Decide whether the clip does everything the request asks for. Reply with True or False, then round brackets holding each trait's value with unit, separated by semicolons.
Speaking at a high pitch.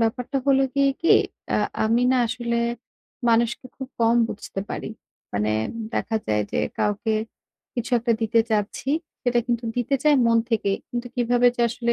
True (235 Hz)